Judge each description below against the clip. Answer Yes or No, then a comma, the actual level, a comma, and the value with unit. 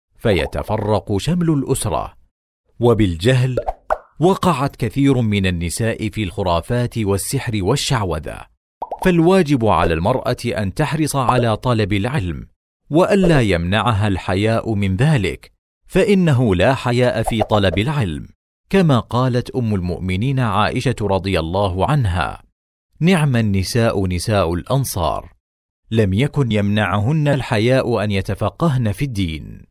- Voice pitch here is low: Yes, low, 115 Hz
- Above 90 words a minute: Yes, average, 105 wpm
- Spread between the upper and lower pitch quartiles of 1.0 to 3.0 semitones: No, average, 5.3 semitones